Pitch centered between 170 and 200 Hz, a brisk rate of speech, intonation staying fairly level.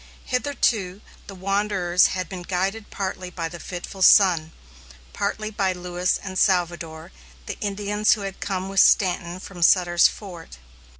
No: medium, 185 Hz; average, 140 wpm; narrow, 2.2 semitones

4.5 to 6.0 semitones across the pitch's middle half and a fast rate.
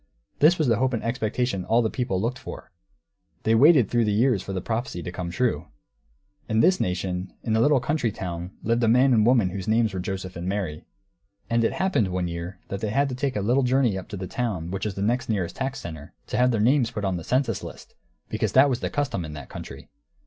Yes: average, 5.2 semitones; fast, 245 wpm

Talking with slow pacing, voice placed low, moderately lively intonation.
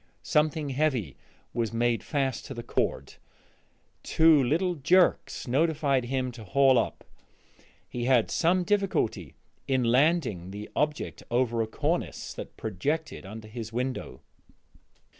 Yes: slow, 125 wpm; low, 130 Hz; average, 4.7 semitones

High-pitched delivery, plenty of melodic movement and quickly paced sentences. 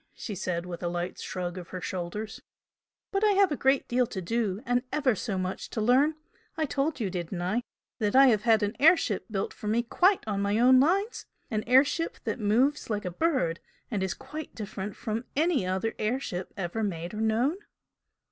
Yes: high, 220 Hz; wide, 6.0 semitones; fast, 210 wpm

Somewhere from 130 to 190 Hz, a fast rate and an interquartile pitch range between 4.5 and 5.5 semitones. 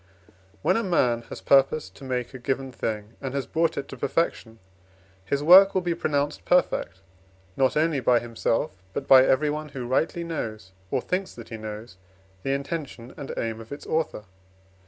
No: low, 135 Hz; average, 175 wpm; average, 4.8 semitones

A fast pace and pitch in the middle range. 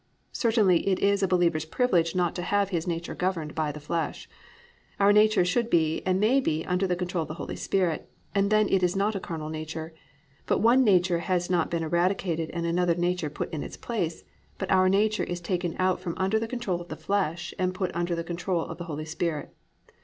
Yes: fast, 220 wpm; medium, 180 Hz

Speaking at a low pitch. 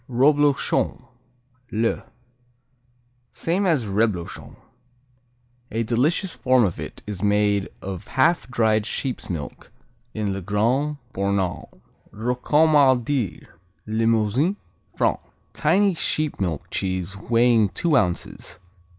Yes: low, 115 Hz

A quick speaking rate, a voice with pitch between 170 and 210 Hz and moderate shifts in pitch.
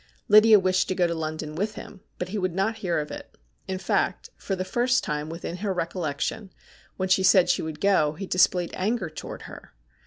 Yes: fast, 210 wpm; medium, 185 Hz; average, 3.3 semitones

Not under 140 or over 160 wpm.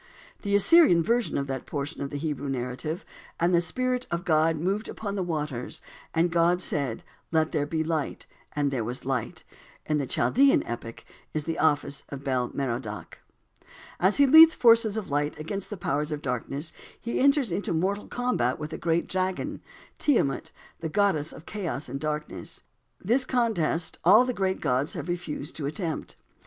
No: average, 175 wpm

